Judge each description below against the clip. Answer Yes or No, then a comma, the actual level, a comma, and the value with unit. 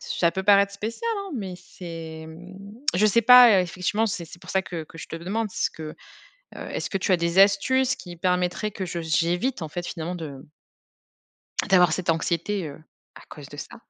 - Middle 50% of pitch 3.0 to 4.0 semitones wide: Yes, average, 3.6 semitones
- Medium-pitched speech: Yes, medium, 180 Hz